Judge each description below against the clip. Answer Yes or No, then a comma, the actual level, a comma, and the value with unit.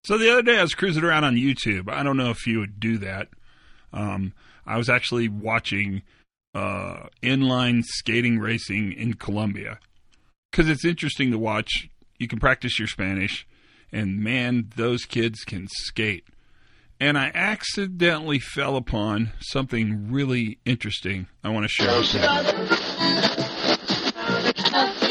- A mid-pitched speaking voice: No, low, 115 Hz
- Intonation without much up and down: No, average, 4.1 semitones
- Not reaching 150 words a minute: Yes, average, 140 wpm